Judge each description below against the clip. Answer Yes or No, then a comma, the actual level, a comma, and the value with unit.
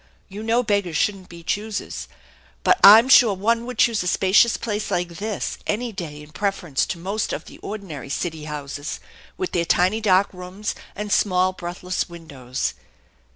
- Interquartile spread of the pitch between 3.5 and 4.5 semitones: Yes, average, 3.9 semitones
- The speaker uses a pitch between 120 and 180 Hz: No, high, 190 Hz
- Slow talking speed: No, average, 165 wpm